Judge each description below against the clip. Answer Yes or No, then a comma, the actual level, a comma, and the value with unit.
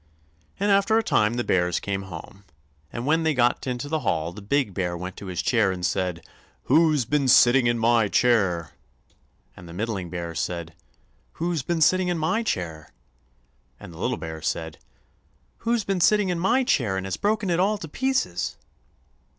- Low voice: Yes, low, 120 Hz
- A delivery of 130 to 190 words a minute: Yes, average, 185 wpm